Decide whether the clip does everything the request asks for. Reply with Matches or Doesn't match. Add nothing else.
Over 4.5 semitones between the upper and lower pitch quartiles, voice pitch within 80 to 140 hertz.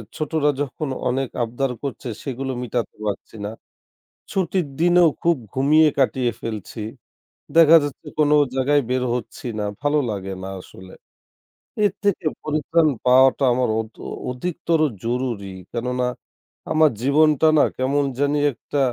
Doesn't match